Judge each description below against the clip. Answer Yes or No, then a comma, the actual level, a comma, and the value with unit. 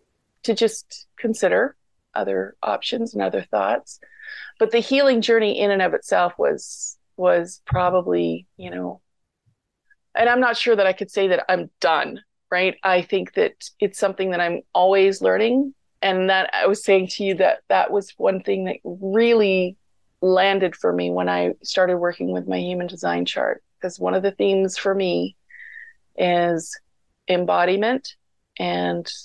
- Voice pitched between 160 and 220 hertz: Yes, high, 190 Hz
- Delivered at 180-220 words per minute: No, average, 160 wpm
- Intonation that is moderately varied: Yes, average, 4.6 semitones